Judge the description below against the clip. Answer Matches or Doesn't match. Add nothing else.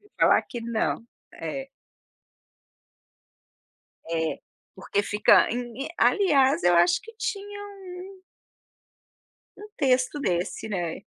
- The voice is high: Matches